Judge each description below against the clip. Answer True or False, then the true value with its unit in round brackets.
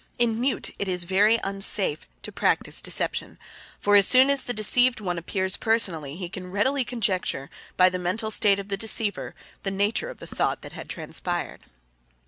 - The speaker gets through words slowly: False (180 wpm)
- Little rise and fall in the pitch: False (3.6 semitones)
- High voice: True (200 Hz)